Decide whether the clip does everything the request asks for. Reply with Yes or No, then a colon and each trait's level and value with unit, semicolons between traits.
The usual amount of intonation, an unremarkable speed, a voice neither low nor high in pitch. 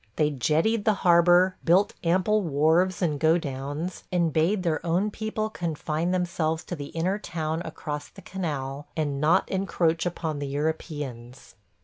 Yes: average, 3.3 semitones; average, 150 wpm; medium, 165 Hz